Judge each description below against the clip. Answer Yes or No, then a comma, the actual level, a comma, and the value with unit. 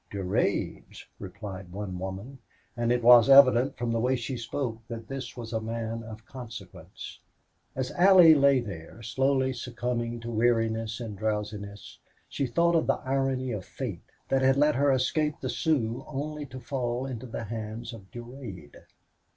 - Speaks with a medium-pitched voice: No, low, 120 Hz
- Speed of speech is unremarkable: Yes, average, 160 wpm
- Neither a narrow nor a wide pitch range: Yes, average, 3.2 semitones